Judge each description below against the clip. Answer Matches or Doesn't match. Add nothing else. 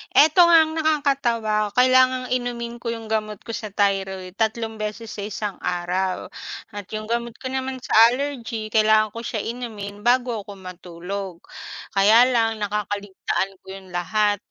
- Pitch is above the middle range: Matches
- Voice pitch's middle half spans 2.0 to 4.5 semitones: Matches